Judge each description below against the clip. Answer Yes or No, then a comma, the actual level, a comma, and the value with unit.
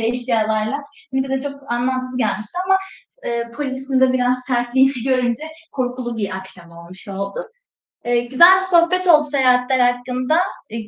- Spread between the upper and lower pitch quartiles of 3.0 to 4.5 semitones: No, narrow, 2.4 semitones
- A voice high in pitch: Yes, very high, 250 Hz